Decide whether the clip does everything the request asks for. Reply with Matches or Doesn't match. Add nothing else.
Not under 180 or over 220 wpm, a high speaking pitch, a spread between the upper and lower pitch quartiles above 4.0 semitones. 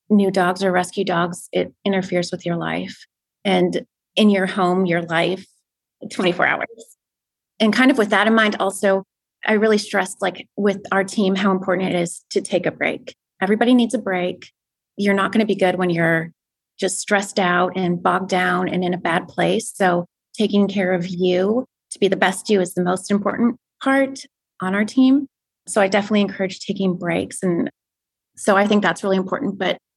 Doesn't match